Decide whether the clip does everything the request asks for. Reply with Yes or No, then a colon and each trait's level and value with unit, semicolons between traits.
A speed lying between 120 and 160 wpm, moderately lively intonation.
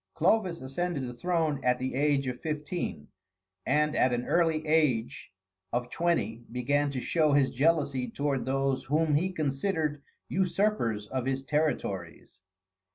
Yes: average, 140 wpm; average, 4.0 semitones